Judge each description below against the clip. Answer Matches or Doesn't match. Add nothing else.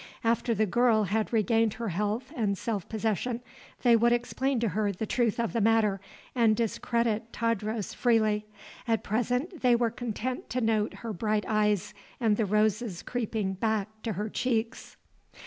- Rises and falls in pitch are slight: Matches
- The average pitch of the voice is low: Doesn't match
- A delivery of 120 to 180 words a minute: Matches